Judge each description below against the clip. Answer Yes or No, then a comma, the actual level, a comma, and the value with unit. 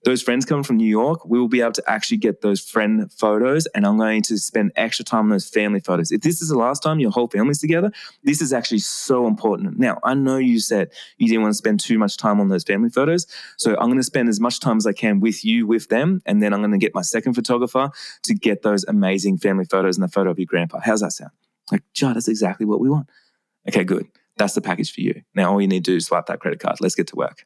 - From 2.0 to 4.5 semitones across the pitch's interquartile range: No, wide, 5.5 semitones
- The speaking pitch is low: Yes, low, 115 Hz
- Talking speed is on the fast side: Yes, fast, 280 wpm